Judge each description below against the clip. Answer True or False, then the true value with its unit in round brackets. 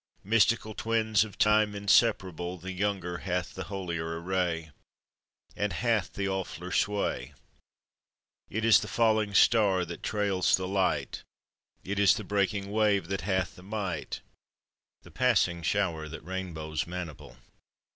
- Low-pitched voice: True (95 Hz)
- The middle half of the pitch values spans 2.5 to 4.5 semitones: True (2.9 semitones)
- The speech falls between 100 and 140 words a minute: True (135 wpm)